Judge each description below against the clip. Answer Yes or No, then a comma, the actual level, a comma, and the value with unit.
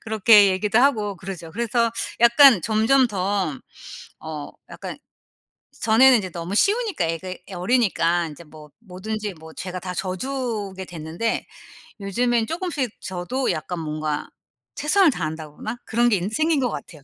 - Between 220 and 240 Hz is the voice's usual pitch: No, high, 205 Hz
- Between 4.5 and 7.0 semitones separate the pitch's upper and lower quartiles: Yes, wide, 5.5 semitones